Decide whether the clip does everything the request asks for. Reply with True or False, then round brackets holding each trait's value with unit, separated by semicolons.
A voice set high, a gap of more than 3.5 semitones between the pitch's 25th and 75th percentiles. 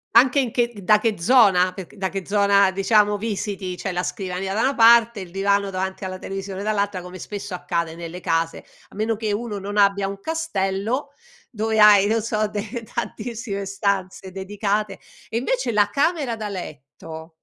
False (200 Hz; 2.7 semitones)